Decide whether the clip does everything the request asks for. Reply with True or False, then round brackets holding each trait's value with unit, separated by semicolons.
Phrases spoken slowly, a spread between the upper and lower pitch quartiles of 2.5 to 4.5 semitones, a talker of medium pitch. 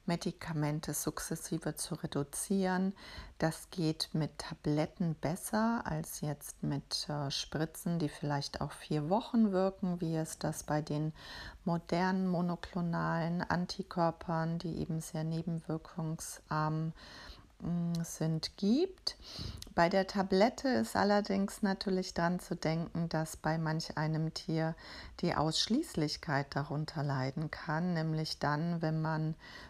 True (115 wpm; 2.8 semitones; 165 Hz)